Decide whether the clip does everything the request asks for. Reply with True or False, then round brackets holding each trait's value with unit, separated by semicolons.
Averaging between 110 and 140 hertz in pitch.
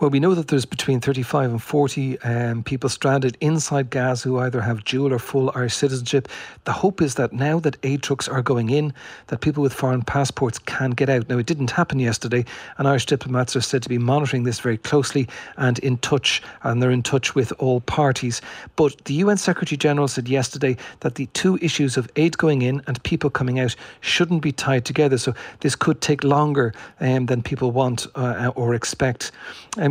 True (135 Hz)